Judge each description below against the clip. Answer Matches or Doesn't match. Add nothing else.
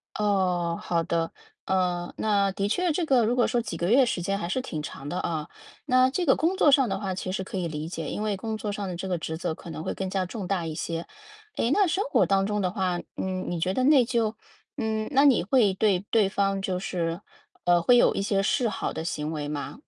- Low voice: Doesn't match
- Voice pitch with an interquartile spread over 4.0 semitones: Matches